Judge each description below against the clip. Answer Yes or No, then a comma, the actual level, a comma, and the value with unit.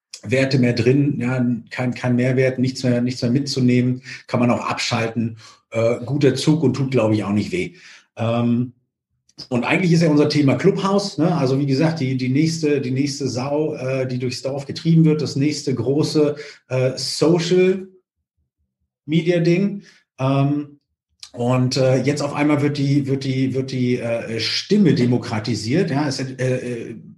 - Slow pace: No, average, 170 wpm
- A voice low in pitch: Yes, low, 130 Hz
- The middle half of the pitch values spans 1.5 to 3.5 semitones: Yes, average, 3.1 semitones